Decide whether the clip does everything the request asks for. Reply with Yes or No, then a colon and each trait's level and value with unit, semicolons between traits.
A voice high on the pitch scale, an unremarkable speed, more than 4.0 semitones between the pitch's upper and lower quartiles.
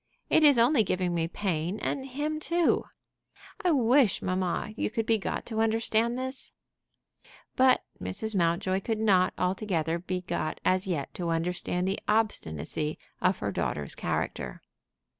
Yes: high, 195 Hz; average, 145 wpm; average, 5.0 semitones